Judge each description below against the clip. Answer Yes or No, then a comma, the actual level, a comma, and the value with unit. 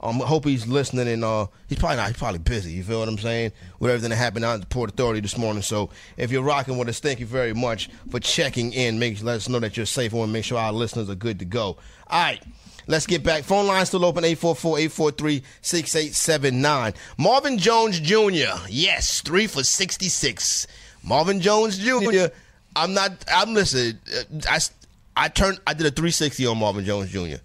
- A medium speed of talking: No, fast, 210 wpm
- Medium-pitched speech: No, low, 130 Hz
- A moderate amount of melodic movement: No, wide, 6.6 semitones